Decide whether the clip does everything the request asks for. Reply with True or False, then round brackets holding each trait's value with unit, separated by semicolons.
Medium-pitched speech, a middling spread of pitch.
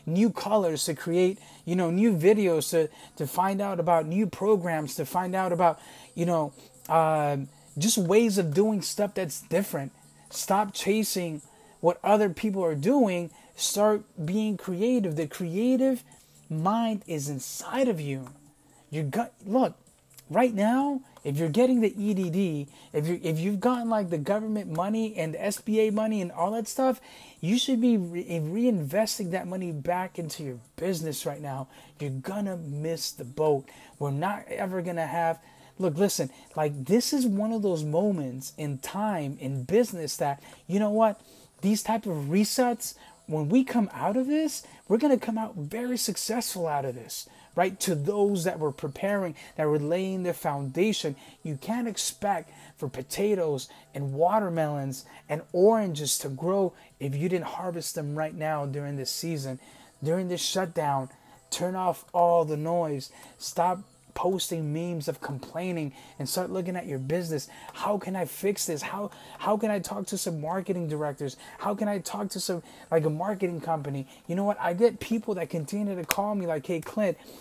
True (175 Hz; 4.9 semitones)